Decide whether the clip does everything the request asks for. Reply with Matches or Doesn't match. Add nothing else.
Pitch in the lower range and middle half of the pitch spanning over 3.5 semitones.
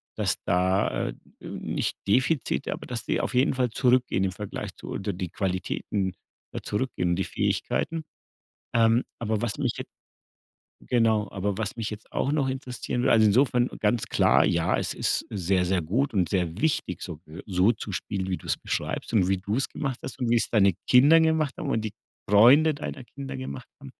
Matches